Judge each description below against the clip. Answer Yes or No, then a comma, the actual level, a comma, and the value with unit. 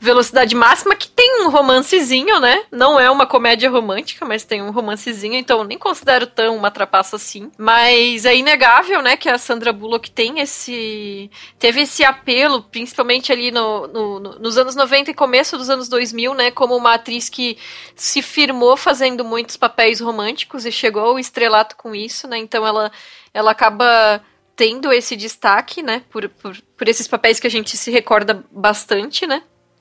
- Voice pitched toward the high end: Yes, high, 240 Hz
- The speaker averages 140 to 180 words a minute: Yes, average, 175 wpm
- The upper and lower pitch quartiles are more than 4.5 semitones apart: No, average, 2.9 semitones